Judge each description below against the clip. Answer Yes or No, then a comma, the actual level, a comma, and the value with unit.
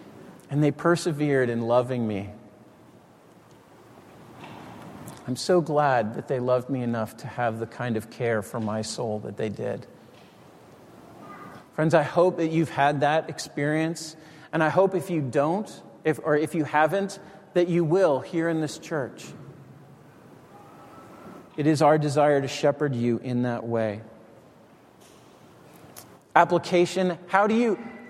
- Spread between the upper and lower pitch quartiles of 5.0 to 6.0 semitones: Yes, wide, 5.4 semitones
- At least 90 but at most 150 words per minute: Yes, average, 140 wpm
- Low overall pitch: No, medium, 150 Hz